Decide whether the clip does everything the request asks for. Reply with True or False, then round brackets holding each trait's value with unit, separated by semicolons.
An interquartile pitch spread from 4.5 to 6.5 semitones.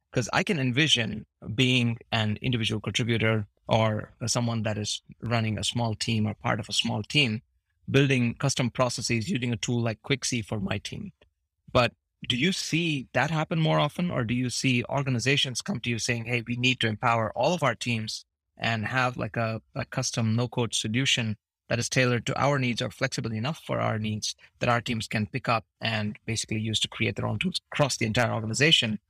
False (2.7 semitones)